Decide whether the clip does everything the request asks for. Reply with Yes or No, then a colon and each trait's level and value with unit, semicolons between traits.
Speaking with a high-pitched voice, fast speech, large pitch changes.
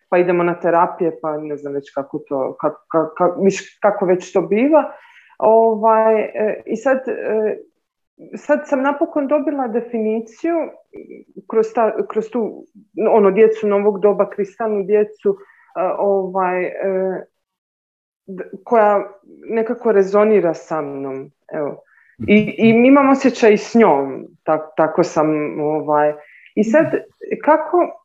No: high, 210 Hz; average, 115 wpm; wide, 5.7 semitones